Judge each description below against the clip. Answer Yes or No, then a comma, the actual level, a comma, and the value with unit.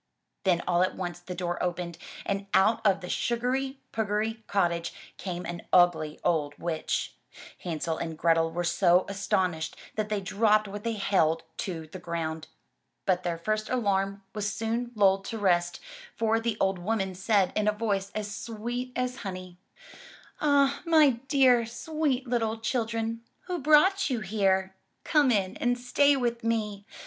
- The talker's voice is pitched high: Yes, high, 205 Hz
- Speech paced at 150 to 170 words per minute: Yes, average, 155 wpm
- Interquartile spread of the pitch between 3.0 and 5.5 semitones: Yes, average, 4.6 semitones